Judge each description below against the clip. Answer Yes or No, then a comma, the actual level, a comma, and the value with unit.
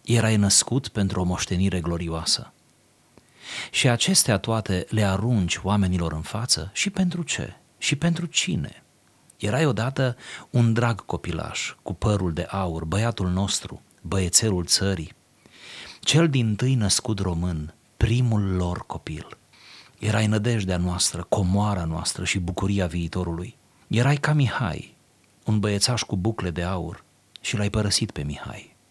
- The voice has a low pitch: Yes, low, 105 Hz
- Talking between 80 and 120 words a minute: No, average, 130 wpm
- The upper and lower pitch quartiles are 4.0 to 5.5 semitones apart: Yes, average, 4.3 semitones